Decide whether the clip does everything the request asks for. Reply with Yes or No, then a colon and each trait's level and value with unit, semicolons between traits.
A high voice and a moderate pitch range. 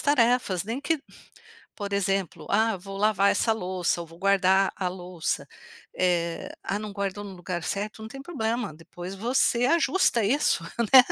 Yes: high, 200 Hz; average, 3.8 semitones